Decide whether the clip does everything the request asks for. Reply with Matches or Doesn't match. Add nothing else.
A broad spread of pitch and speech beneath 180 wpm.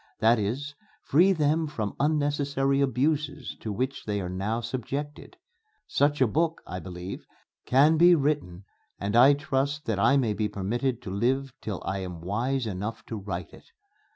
Matches